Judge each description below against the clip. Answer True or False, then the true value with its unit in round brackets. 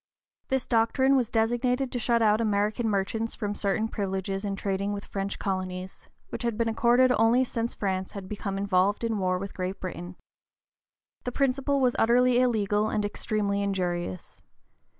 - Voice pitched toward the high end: True (210 Hz)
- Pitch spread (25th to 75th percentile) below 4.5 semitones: True (3.4 semitones)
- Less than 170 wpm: True (160 wpm)